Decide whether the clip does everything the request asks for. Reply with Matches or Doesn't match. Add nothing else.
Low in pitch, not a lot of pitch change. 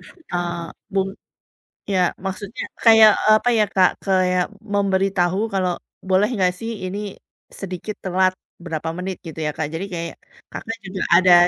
Doesn't match